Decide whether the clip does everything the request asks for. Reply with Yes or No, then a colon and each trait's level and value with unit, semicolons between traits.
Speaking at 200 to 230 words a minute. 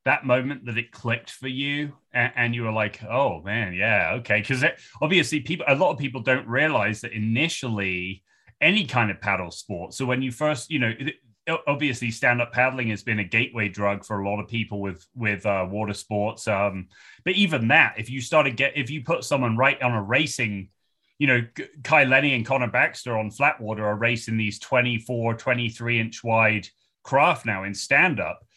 Yes: fast, 205 wpm